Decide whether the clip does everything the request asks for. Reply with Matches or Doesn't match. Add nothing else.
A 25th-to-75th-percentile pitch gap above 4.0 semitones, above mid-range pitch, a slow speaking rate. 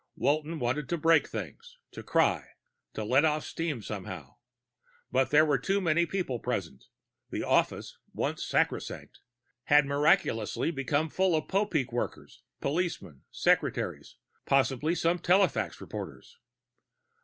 Doesn't match